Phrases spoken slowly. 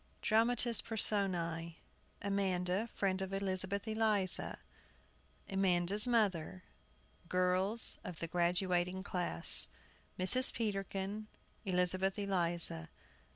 Yes: slow, 80 wpm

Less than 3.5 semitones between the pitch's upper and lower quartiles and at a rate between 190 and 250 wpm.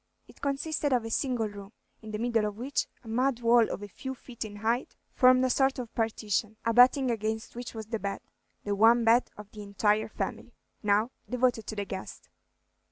Yes: average, 2.9 semitones; average, 200 wpm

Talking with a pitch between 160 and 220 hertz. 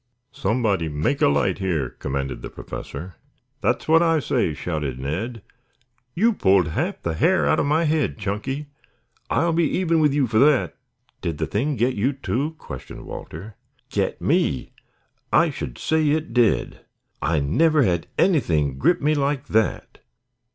No: low, 115 Hz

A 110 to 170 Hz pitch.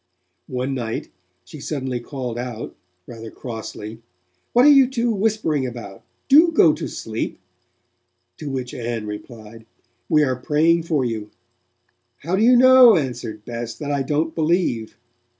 Yes: low, 135 Hz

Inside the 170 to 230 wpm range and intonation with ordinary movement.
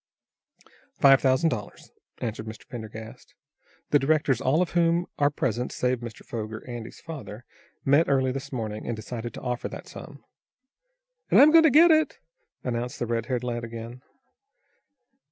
No: average, 155 wpm; average, 3.8 semitones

